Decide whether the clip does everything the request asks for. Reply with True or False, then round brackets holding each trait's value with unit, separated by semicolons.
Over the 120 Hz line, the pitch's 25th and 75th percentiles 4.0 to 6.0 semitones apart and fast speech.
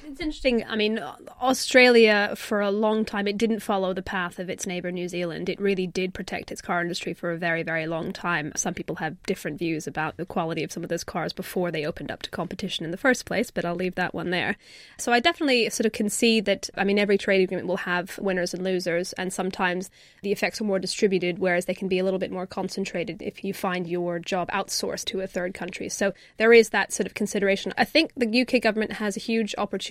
False (190 Hz; 3.0 semitones; 245 wpm)